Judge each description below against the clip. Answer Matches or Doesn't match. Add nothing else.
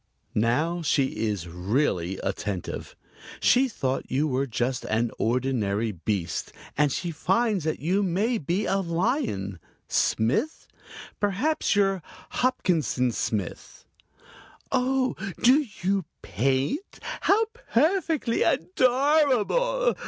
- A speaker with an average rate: Doesn't match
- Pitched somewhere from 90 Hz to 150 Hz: Doesn't match